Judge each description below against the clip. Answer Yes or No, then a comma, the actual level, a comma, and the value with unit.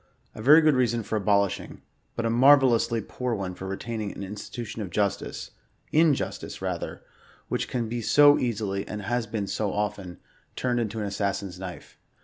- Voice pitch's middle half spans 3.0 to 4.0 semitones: Yes, average, 3.3 semitones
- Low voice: Yes, low, 110 Hz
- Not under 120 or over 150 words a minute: No, average, 170 wpm